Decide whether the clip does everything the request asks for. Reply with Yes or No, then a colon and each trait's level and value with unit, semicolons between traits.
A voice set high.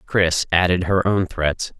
No: very low, 90 Hz